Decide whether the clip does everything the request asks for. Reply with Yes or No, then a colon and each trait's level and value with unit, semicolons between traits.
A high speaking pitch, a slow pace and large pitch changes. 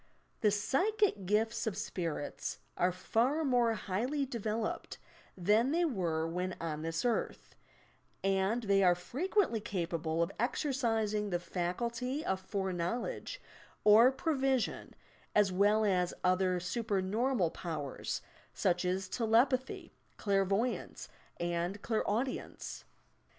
No: high, 205 Hz; slow, 115 wpm; average, 4.9 semitones